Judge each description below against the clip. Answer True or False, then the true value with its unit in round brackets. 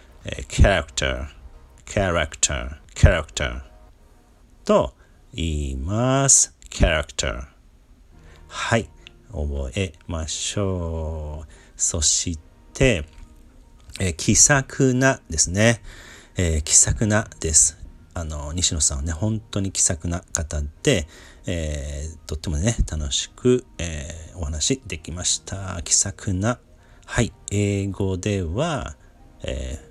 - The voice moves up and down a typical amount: True (4.4 semitones)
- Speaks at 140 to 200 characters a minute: False (210 characters per minute)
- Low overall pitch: True (85 Hz)